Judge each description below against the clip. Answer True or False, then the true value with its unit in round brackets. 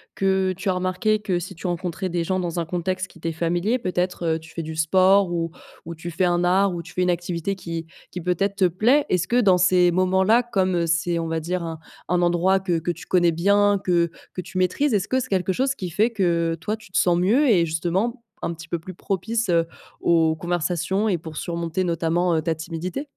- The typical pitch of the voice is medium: True (180 Hz)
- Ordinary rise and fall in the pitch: False (2.3 semitones)